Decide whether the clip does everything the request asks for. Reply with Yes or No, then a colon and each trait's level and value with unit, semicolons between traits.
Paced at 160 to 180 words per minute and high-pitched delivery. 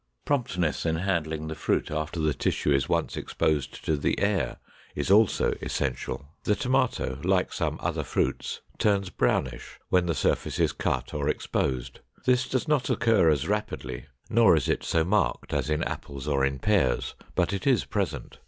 No: average, 170 wpm; very low, 85 Hz